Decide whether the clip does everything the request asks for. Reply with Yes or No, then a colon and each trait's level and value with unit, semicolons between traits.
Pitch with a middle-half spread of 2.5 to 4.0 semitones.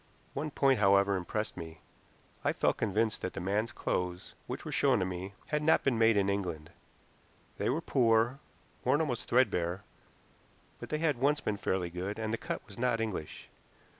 No: average, 5.2 semitones